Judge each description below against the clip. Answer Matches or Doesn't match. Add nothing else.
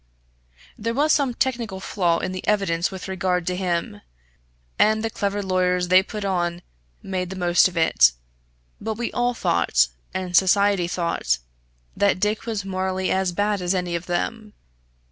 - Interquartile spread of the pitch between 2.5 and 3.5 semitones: Matches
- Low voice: Doesn't match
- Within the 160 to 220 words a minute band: Matches